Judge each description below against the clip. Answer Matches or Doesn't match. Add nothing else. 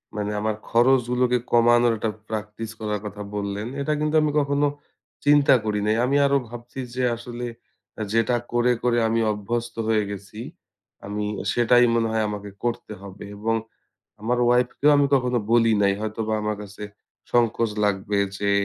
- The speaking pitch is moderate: Doesn't match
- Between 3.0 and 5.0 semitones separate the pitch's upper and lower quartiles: Doesn't match